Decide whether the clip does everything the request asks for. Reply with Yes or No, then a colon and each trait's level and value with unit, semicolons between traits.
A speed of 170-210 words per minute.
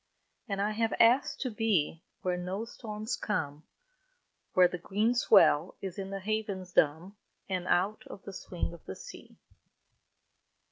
No: average, 150 wpm